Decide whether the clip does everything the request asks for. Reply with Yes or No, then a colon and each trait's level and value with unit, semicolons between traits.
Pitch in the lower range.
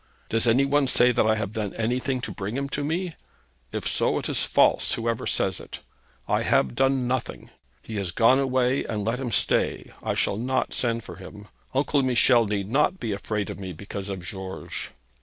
Yes: low, 115 Hz